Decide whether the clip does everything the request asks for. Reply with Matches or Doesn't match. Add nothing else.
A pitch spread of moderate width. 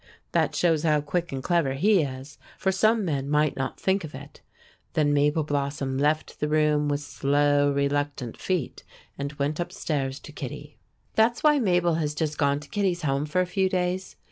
Matches